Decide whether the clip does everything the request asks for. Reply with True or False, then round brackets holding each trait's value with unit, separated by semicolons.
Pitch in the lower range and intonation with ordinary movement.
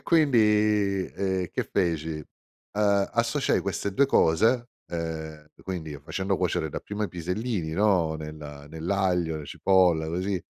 True (95 Hz; 4.2 semitones)